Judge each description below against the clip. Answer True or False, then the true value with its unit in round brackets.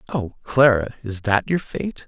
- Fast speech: False (175 wpm)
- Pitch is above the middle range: False (120 Hz)